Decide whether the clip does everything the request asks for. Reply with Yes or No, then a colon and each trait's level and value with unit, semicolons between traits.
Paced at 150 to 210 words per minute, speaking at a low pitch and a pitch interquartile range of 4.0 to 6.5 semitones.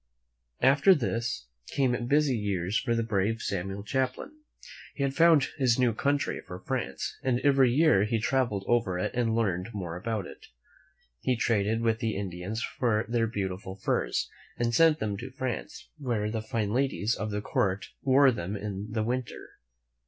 Yes: average, 165 wpm; low, 115 Hz; average, 4.3 semitones